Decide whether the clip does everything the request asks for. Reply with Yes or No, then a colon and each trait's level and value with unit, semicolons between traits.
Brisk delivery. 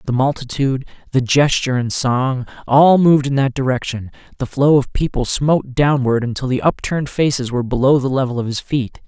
No: average, 185 wpm